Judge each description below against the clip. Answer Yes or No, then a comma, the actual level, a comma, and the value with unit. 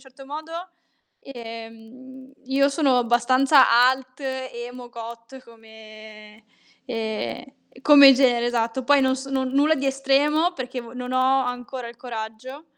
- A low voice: No, very high, 255 Hz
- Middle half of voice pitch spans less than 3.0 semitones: Yes, narrow, 2.5 semitones